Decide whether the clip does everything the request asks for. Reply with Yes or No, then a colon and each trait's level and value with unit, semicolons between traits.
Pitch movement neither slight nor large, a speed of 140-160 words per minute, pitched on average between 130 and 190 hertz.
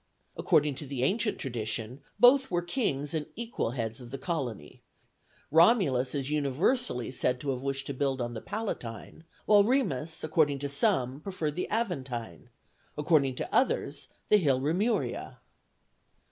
No: wide, 5.8 semitones; average, 150 wpm; medium, 140 Hz